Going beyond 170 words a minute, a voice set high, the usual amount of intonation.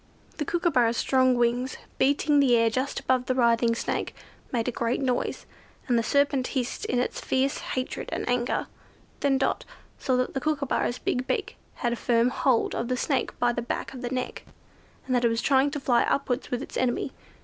No: average, 200 wpm; very high, 255 Hz; narrow, 2.0 semitones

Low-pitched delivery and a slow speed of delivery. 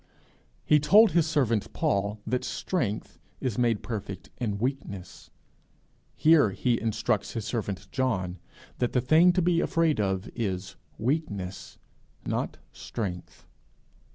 Yes: low, 115 Hz; slow, 125 wpm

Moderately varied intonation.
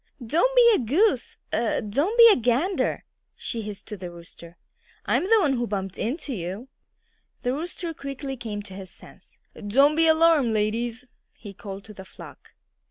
No: wide, 7.3 semitones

